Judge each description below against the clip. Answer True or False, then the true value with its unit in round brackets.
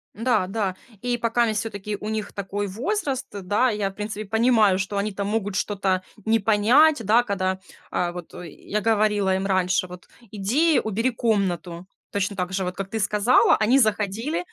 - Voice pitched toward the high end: True (210 Hz)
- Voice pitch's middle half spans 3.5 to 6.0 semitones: False (2.8 semitones)